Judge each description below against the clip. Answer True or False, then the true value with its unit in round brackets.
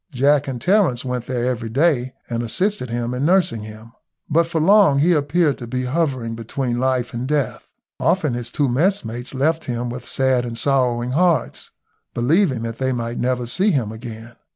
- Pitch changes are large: False (4.1 semitones)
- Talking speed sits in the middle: True (175 wpm)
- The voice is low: True (130 Hz)